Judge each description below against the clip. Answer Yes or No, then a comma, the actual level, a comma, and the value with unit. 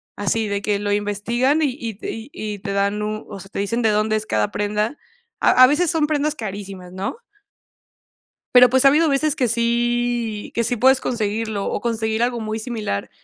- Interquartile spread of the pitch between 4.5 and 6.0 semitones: No, average, 3.1 semitones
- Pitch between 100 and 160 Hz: No, high, 220 Hz